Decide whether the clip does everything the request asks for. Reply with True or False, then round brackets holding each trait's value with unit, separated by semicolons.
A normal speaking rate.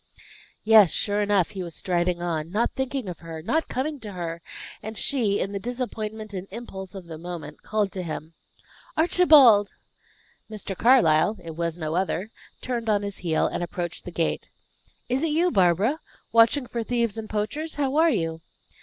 True (175 wpm)